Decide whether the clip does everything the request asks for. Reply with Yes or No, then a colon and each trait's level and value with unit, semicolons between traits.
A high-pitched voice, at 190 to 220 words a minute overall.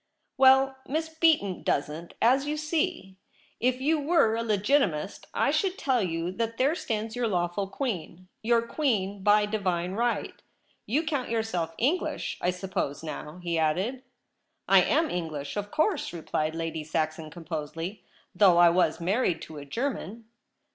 No: high, 205 Hz; average, 160 wpm